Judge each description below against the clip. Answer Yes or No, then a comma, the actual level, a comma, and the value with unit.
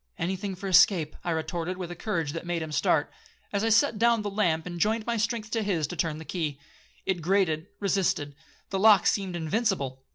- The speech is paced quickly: Yes, fast, 215 wpm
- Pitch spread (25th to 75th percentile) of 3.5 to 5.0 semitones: Yes, average, 4.3 semitones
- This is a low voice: No, medium, 185 Hz